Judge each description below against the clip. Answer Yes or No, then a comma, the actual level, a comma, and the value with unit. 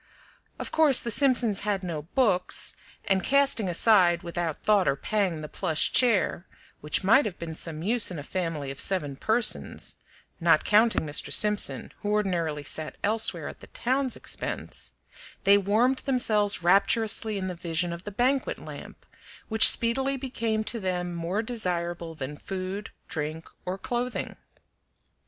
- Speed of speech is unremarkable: Yes, average, 155 wpm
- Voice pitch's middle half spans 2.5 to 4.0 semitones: No, average, 4.9 semitones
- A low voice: No, high, 195 Hz